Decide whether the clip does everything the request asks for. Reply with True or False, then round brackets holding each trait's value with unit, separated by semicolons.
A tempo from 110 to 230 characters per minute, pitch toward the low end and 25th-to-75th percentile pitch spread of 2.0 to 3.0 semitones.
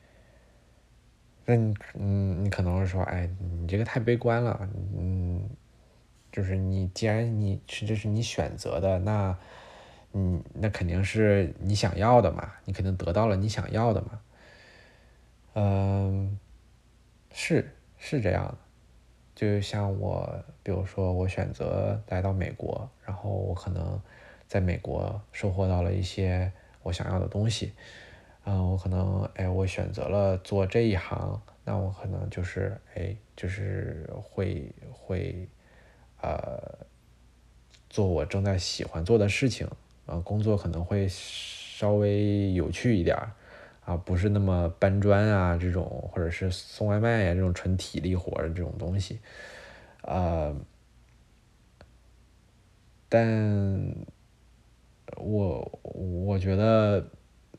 True (185 characters per minute; 95 Hz; 2.4 semitones)